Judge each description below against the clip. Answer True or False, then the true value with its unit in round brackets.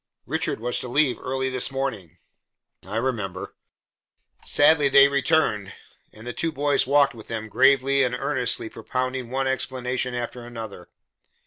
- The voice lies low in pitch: True (130 Hz)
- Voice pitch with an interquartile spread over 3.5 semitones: False (2.8 semitones)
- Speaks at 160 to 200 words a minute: False (140 wpm)